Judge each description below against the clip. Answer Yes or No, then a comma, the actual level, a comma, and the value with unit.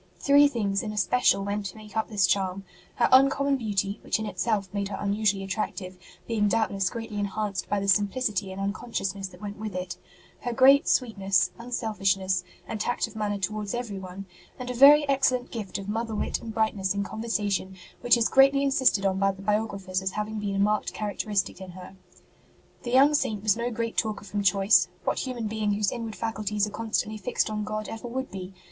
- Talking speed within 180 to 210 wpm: Yes, average, 200 wpm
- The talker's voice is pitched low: No, high, 210 Hz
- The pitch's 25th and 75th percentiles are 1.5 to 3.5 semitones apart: Yes, average, 2.7 semitones